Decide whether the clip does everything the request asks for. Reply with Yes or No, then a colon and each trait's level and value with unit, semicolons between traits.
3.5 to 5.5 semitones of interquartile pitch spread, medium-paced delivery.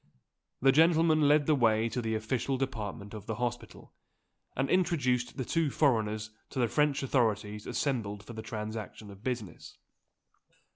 Yes: average, 4.2 semitones; average, 150 wpm